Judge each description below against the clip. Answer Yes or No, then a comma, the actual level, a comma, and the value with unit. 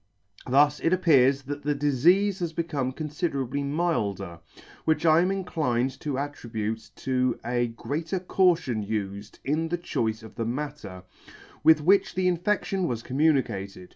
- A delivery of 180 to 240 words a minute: No, average, 145 wpm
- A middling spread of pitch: No, wide, 5.7 semitones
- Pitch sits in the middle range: Yes, medium, 145 Hz